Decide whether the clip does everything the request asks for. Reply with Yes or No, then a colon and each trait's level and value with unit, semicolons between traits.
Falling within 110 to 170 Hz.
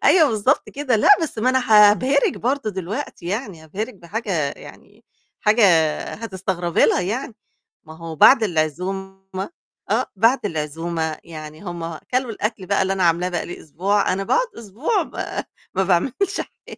No: high, 195 Hz